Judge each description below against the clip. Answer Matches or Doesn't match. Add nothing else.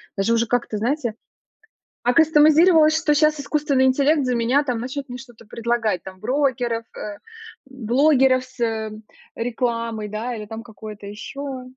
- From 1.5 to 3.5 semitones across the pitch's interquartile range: Doesn't match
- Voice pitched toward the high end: Matches